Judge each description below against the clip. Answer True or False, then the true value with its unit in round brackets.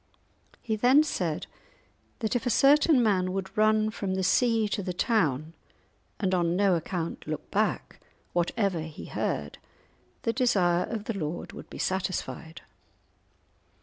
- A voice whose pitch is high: True (195 Hz)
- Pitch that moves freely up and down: False (4.4 semitones)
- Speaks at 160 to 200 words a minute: False (145 wpm)